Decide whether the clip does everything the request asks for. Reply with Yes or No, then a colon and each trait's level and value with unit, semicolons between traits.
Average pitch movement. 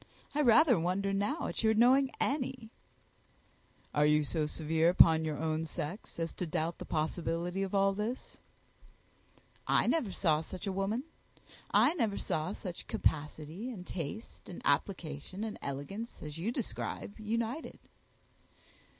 No: wide, 5.8 semitones